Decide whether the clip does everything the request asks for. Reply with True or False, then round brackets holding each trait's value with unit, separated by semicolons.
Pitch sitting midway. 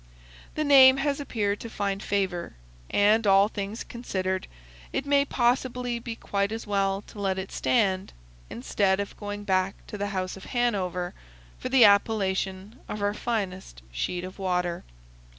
False (200 Hz)